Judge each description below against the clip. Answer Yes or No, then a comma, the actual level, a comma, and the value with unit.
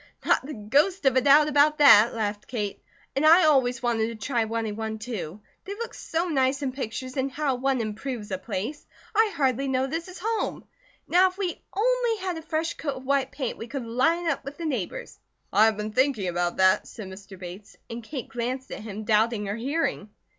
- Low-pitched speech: No, very high, 260 Hz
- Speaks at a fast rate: Yes, fast, 210 wpm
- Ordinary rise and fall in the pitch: No, wide, 5.8 semitones